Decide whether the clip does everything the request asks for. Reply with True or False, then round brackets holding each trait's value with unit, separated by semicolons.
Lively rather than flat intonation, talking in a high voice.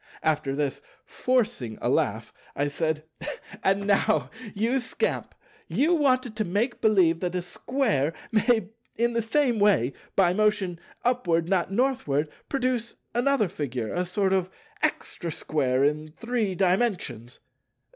True (7.0 semitones; 195 Hz)